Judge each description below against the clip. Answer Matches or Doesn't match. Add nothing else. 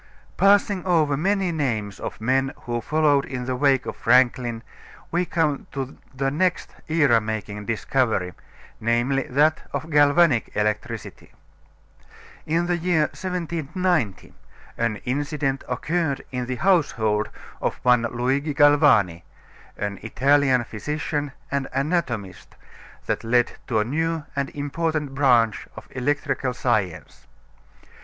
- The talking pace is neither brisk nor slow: Doesn't match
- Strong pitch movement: Doesn't match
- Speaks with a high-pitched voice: Doesn't match